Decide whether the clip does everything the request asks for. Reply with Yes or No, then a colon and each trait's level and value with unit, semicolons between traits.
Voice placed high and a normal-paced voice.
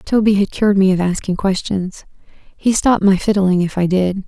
Yes: high, 195 Hz; average, 195 wpm